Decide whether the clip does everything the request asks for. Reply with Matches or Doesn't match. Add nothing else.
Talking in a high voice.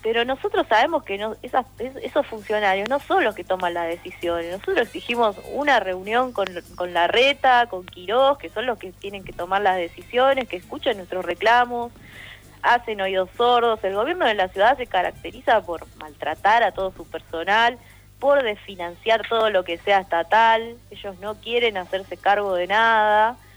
Matches